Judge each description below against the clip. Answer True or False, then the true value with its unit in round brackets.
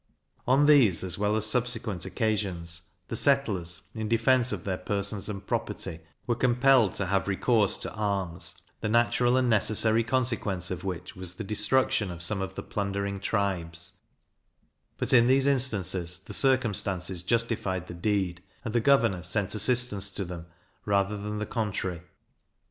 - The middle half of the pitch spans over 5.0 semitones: False (4.0 semitones)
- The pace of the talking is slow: False (155 wpm)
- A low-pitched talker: True (105 Hz)